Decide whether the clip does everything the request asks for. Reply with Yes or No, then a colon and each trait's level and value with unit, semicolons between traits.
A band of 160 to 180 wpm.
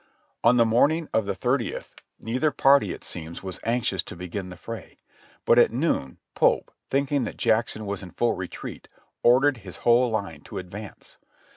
Yes: average, 175 wpm